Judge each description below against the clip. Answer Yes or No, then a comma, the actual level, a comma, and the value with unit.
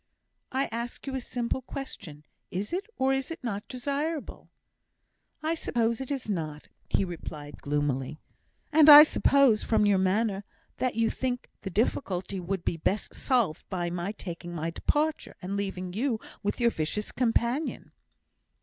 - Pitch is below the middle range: No, high, 215 Hz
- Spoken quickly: No, average, 155 wpm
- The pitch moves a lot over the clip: Yes, wide, 6.5 semitones